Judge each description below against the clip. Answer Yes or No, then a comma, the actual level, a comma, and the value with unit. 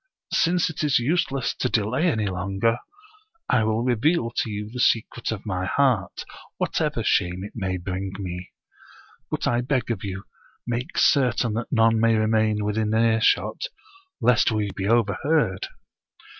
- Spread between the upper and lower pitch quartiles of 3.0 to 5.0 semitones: Yes, average, 3.5 semitones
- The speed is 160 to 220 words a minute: No, average, 150 wpm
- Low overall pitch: Yes, low, 110 Hz